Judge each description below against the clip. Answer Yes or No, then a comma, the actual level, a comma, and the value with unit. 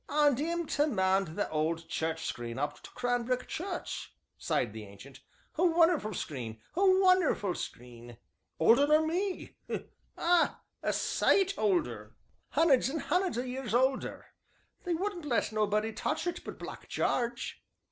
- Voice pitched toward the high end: Yes, high, 245 Hz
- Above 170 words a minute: No, average, 145 wpm